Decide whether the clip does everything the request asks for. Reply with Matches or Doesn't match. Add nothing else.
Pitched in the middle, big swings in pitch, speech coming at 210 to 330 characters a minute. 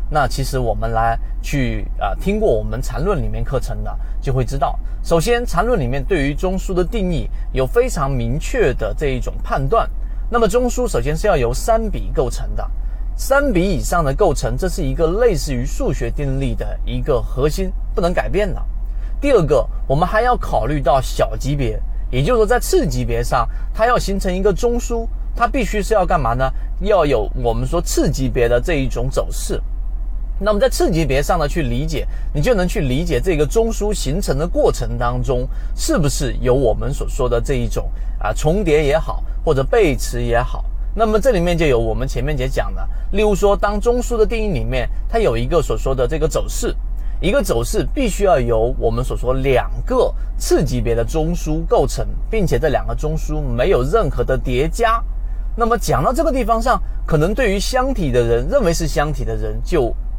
Matches